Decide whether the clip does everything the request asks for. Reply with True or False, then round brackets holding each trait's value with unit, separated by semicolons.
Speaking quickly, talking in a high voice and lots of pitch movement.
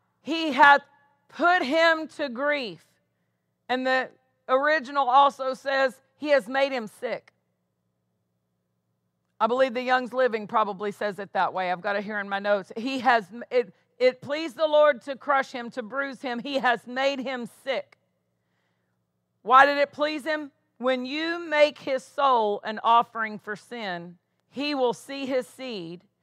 False (160 wpm; 255 Hz; 5.8 semitones)